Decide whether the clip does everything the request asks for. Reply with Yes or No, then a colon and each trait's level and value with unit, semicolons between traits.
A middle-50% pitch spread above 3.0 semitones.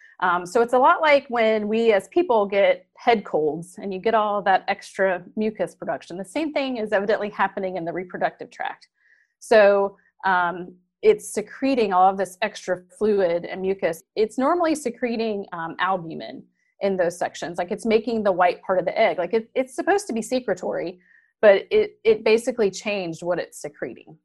Yes: average, 4.5 semitones